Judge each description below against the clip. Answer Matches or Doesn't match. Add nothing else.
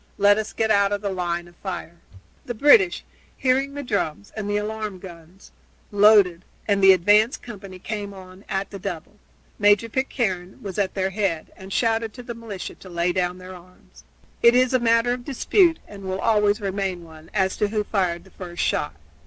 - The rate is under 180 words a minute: Doesn't match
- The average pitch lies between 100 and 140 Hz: Doesn't match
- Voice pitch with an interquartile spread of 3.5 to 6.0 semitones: Doesn't match